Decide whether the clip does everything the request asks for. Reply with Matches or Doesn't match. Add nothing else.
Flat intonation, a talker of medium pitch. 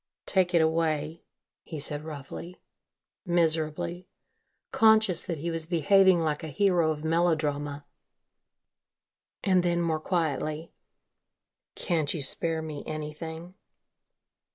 Matches